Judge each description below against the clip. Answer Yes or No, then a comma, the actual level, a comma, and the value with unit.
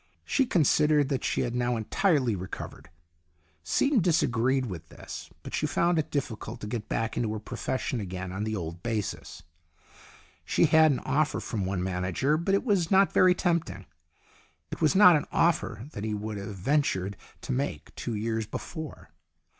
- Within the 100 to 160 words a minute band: No, average, 170 wpm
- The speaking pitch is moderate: No, low, 120 Hz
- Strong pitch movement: Yes, wide, 7.2 semitones